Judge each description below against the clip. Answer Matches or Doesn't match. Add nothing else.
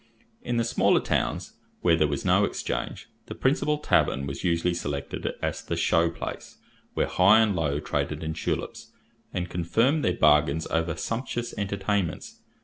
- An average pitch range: Doesn't match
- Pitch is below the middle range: Matches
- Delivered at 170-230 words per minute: Doesn't match